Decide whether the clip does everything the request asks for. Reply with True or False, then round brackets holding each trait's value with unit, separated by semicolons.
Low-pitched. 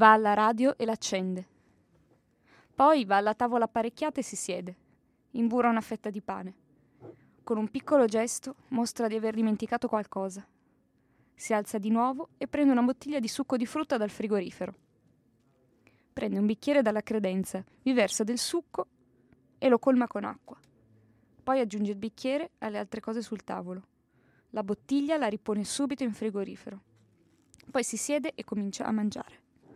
False (220 Hz)